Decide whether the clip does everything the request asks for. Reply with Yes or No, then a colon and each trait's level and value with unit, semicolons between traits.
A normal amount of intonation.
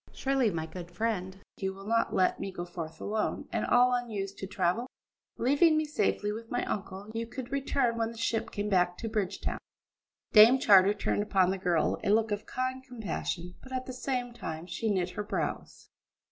Yes: average, 4.5 semitones